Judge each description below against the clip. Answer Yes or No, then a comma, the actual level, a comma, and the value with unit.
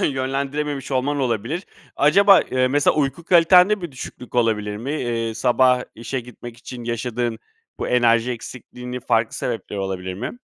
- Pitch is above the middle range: No, low, 125 Hz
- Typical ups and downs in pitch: Yes, average, 3.3 semitones